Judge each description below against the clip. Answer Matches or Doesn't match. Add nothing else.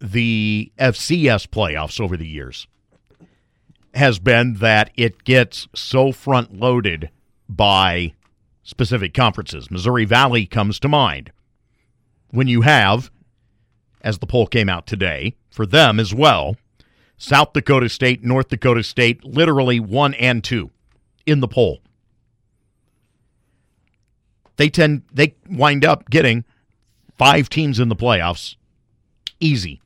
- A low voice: Matches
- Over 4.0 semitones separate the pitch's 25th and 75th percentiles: Doesn't match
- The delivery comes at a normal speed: Doesn't match